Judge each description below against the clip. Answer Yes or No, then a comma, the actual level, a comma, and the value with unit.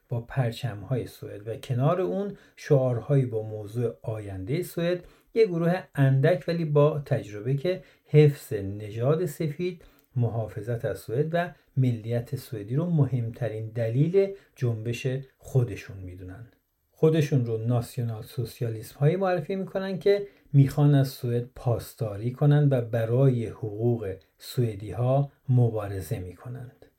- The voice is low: Yes, low, 130 Hz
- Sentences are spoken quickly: No, average, 120 wpm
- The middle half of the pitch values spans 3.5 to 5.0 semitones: Yes, average, 4.6 semitones